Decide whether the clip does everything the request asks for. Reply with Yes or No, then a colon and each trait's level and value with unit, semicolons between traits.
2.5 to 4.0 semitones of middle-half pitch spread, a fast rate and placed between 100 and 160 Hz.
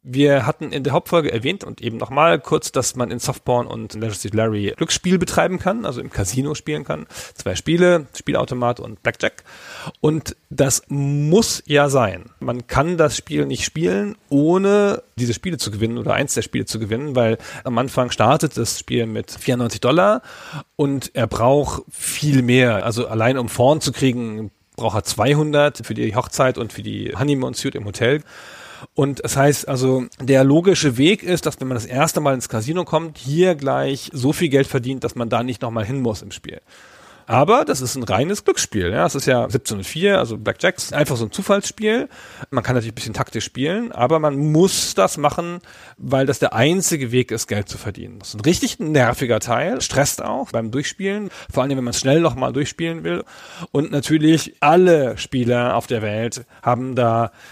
No: average, 4.5 semitones; fast, 195 wpm; low, 135 Hz